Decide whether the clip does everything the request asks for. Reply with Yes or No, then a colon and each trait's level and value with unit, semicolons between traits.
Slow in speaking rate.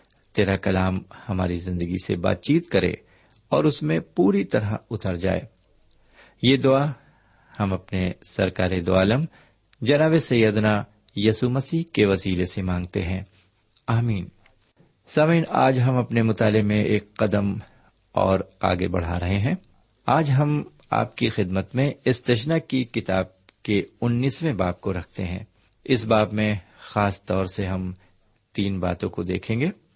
No: average, 145 wpm